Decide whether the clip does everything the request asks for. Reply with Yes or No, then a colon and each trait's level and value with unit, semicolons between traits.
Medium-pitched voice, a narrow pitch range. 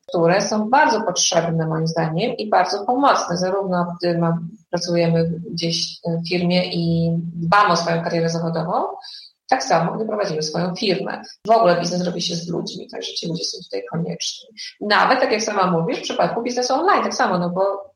No: medium, 180 Hz; average, 4.2 semitones